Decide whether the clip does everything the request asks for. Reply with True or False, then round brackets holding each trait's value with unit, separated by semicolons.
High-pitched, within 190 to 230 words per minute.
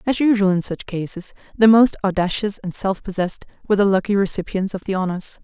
True (195 Hz; 200 wpm)